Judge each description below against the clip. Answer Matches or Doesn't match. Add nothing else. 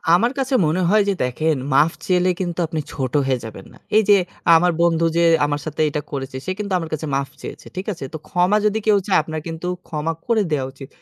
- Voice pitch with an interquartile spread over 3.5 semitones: Matches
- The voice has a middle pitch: Matches